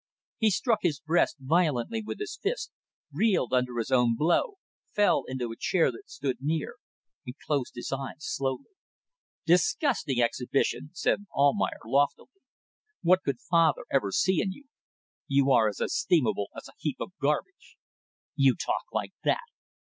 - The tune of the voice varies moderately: No, wide, 6.2 semitones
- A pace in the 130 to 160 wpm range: Yes, average, 150 wpm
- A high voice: No, medium, 140 Hz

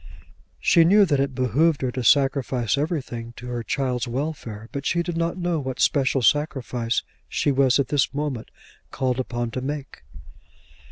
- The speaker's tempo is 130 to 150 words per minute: No, average, 165 wpm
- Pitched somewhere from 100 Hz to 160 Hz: Yes, low, 135 Hz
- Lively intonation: No, average, 3.2 semitones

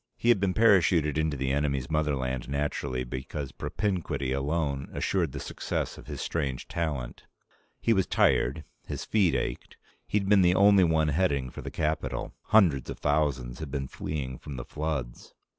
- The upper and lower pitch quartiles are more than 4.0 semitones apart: Yes, average, 4.6 semitones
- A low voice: Yes, very low, 75 Hz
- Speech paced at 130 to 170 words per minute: Yes, average, 165 wpm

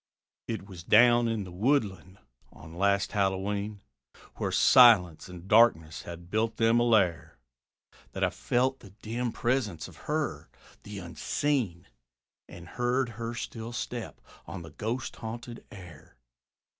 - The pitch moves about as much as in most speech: Yes, average, 4.7 semitones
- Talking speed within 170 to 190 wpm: No, slow, 135 wpm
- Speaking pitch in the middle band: No, low, 105 Hz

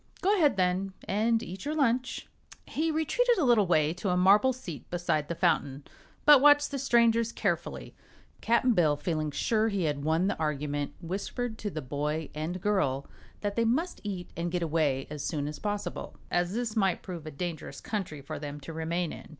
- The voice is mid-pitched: Yes, medium, 180 Hz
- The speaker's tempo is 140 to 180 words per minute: No, average, 190 wpm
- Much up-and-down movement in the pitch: Yes, wide, 6.7 semitones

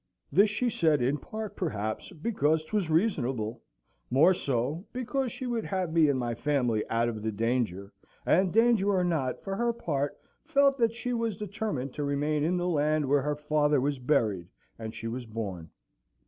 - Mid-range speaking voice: Yes, medium, 150 Hz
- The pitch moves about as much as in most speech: No, wide, 8.3 semitones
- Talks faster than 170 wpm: Yes, average, 180 wpm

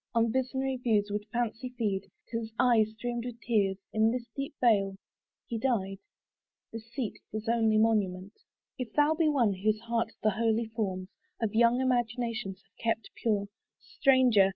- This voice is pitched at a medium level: No, high, 225 Hz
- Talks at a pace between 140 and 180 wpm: Yes, average, 160 wpm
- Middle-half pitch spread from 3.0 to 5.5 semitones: No, narrow, 2.5 semitones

